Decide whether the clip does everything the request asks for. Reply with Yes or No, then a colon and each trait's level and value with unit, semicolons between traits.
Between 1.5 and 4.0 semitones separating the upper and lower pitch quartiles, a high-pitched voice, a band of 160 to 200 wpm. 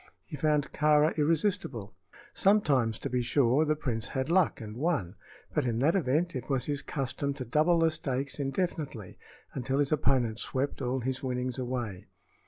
No: average, 3.5 semitones; low, 135 Hz; average, 170 wpm